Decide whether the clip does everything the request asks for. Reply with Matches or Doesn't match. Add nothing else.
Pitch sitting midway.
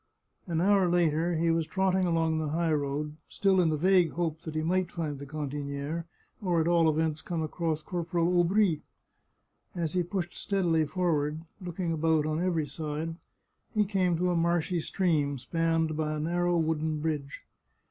Matches